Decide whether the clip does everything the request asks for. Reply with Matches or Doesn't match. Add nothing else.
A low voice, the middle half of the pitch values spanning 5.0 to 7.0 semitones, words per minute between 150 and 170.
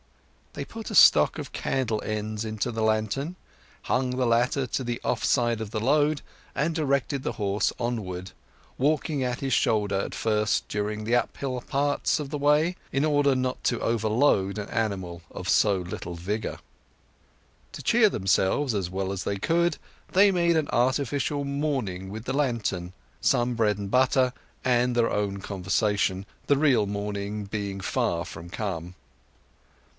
Matches